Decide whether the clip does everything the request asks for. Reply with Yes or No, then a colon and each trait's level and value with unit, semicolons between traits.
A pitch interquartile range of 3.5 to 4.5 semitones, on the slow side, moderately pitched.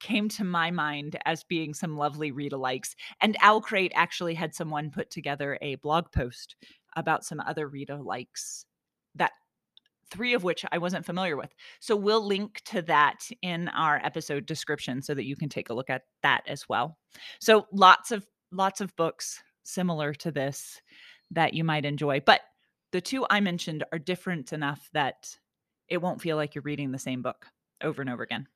No: average, 4.1 semitones; average, 180 wpm; medium, 160 Hz